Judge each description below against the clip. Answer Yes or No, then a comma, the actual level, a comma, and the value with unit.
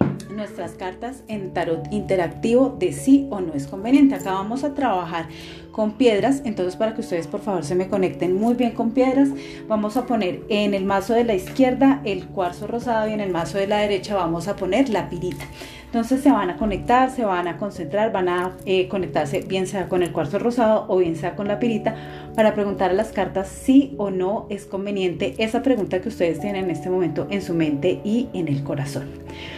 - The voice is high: Yes, high, 200 Hz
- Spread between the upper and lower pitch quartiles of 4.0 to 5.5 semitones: Yes, average, 4.3 semitones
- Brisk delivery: Yes, fast, 215 wpm